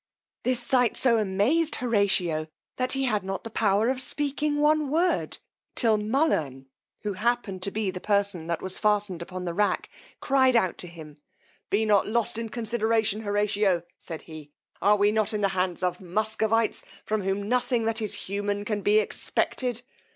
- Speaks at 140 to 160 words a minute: No, average, 175 wpm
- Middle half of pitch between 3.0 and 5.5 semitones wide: Yes, average, 3.6 semitones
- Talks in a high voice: Yes, high, 210 Hz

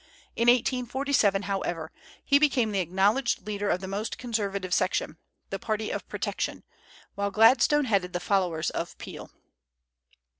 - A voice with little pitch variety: No, average, 3.9 semitones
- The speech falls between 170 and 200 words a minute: No, average, 140 wpm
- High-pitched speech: Yes, high, 210 Hz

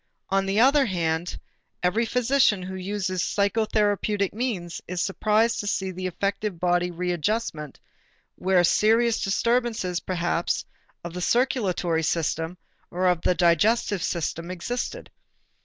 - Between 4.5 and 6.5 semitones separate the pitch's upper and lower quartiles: No, average, 3.7 semitones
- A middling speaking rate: No, slow, 120 wpm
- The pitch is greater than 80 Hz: Yes, high, 190 Hz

